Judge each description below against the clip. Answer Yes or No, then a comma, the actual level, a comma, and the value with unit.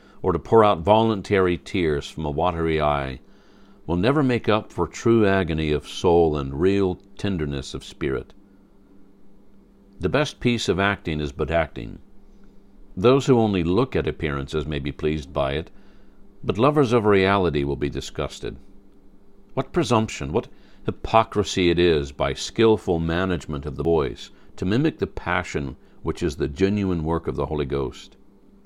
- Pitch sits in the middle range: No, very low, 95 Hz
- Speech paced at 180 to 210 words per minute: No, average, 155 wpm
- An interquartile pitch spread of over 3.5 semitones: Yes, average, 4.5 semitones